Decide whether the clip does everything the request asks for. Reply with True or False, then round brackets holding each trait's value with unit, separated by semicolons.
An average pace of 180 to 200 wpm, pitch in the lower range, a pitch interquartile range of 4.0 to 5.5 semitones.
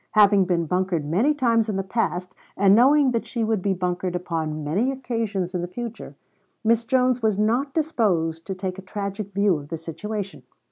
False (190 wpm; 200 Hz; 4.3 semitones)